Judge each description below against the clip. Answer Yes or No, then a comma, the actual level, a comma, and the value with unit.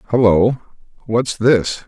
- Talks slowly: Yes, slow, 95 wpm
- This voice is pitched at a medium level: No, low, 115 Hz